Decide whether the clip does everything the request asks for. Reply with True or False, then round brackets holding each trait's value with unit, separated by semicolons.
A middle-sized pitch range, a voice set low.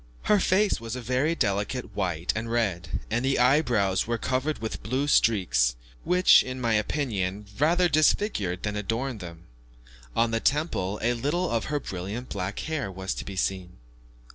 False (6.0 semitones; 115 Hz)